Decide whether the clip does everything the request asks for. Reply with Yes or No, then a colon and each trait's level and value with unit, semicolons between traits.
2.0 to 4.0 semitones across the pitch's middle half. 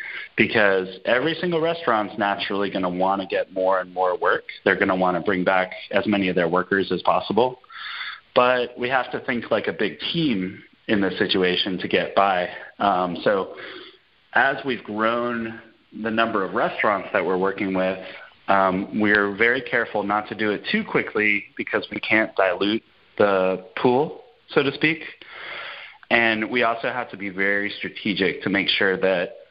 Yes: average, 3.2 semitones